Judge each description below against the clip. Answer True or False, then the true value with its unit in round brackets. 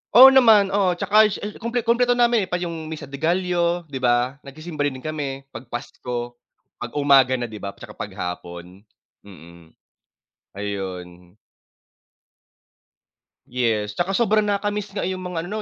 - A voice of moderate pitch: True (155 Hz)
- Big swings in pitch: True (8.6 semitones)